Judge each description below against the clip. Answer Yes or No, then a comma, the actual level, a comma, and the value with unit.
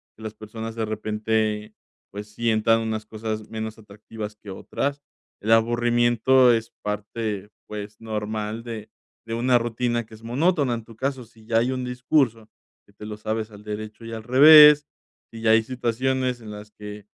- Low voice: Yes, low, 110 Hz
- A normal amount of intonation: No, narrow, 2.0 semitones